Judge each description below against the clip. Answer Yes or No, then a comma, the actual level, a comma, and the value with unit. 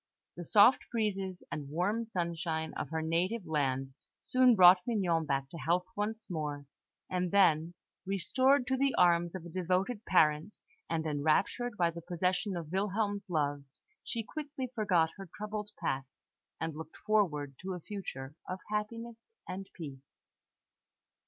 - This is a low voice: No, medium, 180 Hz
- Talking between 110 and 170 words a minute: Yes, average, 145 wpm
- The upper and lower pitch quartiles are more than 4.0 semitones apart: Yes, average, 4.8 semitones